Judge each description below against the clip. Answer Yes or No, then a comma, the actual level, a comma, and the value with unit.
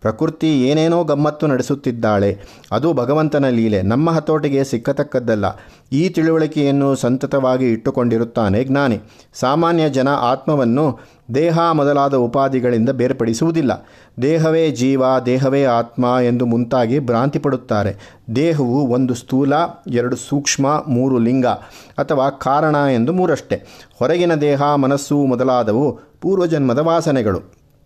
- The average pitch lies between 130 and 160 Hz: Yes, low, 135 Hz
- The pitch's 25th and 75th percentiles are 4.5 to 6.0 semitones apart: No, average, 3.6 semitones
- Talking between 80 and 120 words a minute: Yes, average, 100 wpm